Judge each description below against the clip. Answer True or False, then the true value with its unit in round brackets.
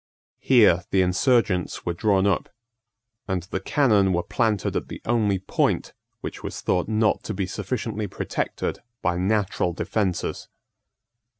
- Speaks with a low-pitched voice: True (100 Hz)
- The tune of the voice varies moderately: True (3.0 semitones)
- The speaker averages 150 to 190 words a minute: False (135 wpm)